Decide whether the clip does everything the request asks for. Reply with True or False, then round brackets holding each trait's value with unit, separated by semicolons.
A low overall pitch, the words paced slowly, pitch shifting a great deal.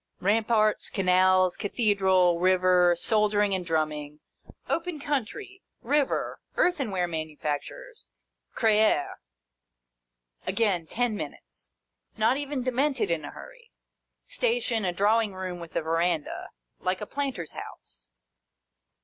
False (205 Hz; 105 wpm; 6.0 semitones)